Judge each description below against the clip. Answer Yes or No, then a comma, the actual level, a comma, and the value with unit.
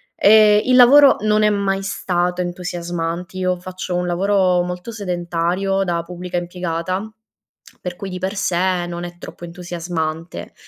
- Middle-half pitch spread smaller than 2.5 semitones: Yes, narrow, 1.9 semitones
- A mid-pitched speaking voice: Yes, medium, 180 Hz